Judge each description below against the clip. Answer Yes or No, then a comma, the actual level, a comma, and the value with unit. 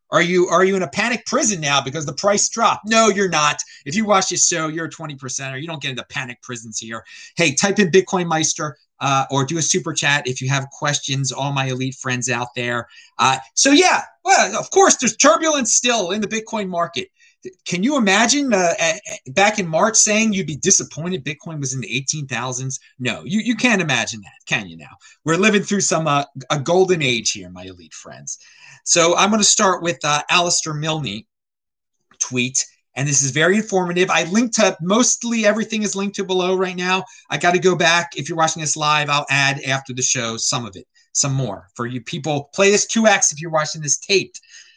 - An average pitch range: No, wide, 6.7 semitones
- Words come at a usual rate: No, fast, 215 wpm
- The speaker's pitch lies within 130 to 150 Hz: No, medium, 165 Hz